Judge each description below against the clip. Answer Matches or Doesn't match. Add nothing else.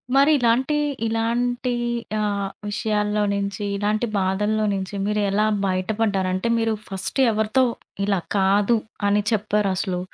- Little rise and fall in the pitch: Matches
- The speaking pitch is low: Doesn't match